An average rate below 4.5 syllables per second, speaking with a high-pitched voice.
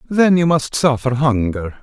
No: 4.1 syllables/s; medium, 140 Hz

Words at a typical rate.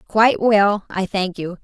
Yes: average, 185 wpm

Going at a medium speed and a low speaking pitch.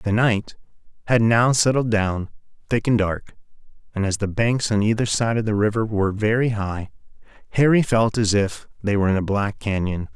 Yes: average, 190 wpm; low, 105 Hz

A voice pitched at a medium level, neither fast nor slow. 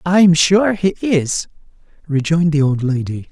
Yes: medium, 165 Hz; average, 145 wpm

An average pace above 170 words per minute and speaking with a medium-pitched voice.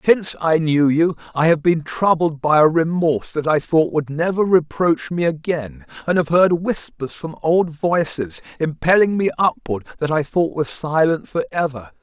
Yes: average, 180 wpm; medium, 160 Hz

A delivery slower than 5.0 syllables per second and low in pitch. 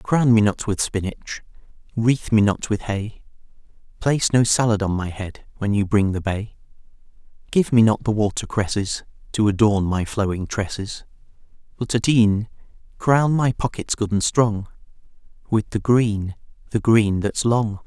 Yes: 4.6 syllables/s; low, 110 Hz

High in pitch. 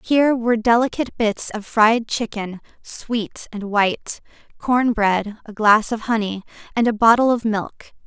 Yes: high, 225 Hz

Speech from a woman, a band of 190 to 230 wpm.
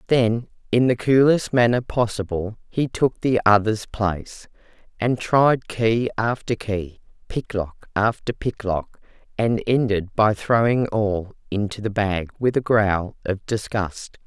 No: female; slow, 135 wpm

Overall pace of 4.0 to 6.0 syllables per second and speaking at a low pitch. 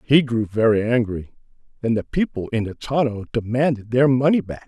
Yes: 5.3 syllables/s; low, 120 Hz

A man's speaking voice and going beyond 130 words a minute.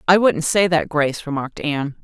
No: female; fast, 205 wpm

